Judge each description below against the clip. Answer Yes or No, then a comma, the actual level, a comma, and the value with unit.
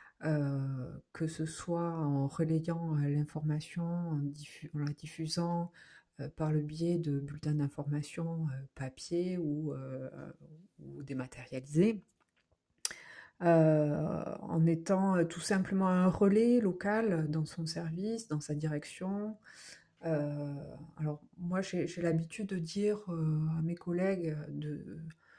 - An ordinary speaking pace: No, slow, 130 wpm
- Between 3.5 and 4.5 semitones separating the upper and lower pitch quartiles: No, average, 2.8 semitones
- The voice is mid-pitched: Yes, medium, 160 Hz